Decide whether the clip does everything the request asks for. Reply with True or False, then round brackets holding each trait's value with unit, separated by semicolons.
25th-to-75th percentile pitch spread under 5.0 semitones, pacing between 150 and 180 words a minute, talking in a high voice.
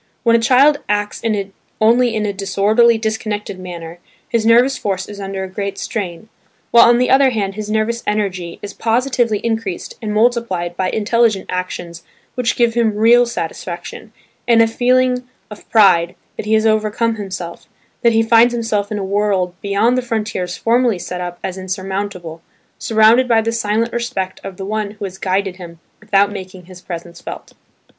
True (3.4 semitones; 175 wpm; 210 Hz)